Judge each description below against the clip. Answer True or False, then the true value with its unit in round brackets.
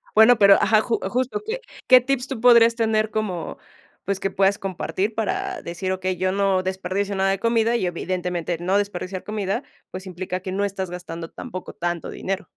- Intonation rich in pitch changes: False (3.3 semitones)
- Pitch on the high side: True (195 Hz)